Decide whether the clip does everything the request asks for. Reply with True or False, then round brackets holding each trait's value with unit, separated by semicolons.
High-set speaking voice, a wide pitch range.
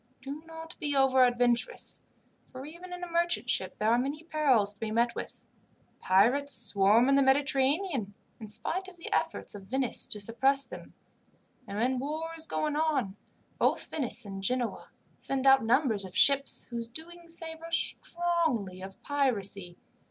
True (270 Hz; 5.8 semitones)